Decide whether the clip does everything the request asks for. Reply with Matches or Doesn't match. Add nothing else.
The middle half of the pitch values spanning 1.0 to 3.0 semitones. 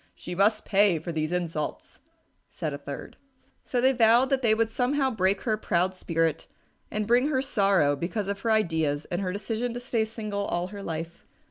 Doesn't match